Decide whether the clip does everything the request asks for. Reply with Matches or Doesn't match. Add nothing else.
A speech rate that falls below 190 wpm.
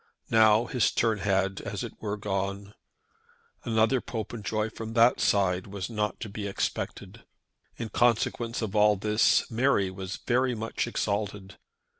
Matches